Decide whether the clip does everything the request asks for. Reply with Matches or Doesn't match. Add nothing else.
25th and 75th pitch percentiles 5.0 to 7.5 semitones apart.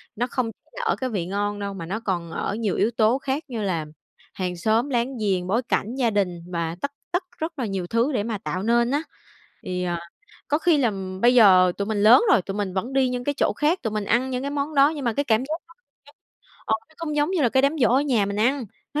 Matches